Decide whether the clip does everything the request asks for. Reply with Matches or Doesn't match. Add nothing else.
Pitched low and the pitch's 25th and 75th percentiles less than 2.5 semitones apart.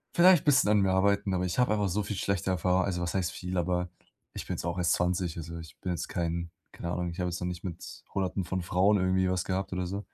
Matches